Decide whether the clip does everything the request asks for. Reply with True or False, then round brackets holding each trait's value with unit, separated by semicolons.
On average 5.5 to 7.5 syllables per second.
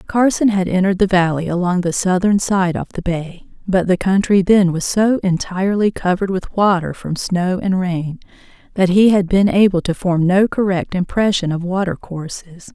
False (4.9 syllables/s)